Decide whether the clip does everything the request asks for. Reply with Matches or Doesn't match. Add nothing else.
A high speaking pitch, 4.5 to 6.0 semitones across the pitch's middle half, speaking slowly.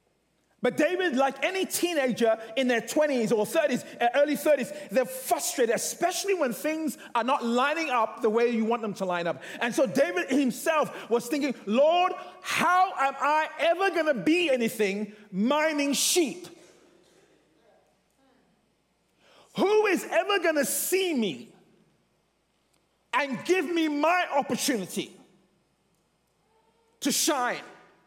Matches